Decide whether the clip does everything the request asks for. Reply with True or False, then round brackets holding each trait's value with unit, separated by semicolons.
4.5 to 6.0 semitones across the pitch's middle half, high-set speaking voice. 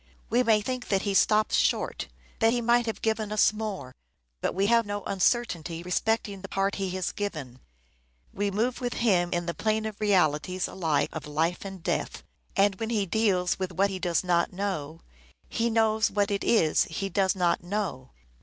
False (3.6 semitones; 195 Hz)